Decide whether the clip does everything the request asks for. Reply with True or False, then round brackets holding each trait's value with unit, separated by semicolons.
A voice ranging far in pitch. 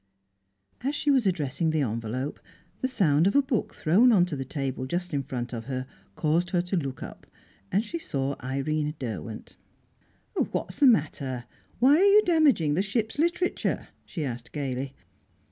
True (8.9 semitones)